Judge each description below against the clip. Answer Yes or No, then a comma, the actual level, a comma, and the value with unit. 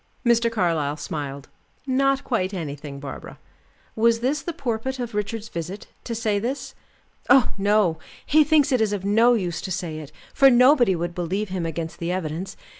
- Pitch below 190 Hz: No, high, 205 Hz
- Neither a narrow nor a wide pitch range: No, wide, 6.2 semitones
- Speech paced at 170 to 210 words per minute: Yes, average, 175 wpm